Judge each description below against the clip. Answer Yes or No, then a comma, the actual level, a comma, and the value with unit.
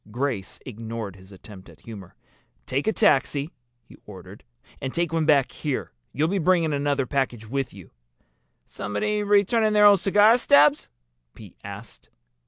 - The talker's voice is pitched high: No, medium, 140 Hz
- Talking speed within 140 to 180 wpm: Yes, average, 150 wpm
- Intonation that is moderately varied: No, wide, 8.9 semitones